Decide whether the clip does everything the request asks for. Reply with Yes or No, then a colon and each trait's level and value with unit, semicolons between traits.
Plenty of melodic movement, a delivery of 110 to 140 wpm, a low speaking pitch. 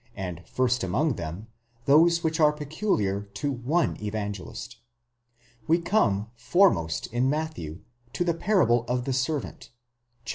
Yes: wide, 7.6 semitones; slow, 135 wpm; low, 130 Hz